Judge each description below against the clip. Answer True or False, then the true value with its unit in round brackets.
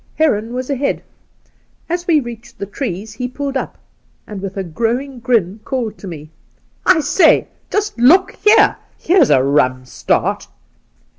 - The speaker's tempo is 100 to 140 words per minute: False (160 wpm)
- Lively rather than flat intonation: True (6.5 semitones)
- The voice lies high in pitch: True (240 Hz)